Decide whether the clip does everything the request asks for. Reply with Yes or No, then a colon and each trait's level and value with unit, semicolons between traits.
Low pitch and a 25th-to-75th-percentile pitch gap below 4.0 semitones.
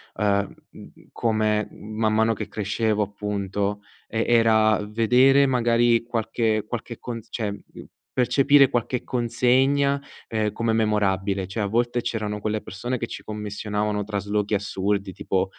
Yes: low, 110 Hz; narrow, 2.4 semitones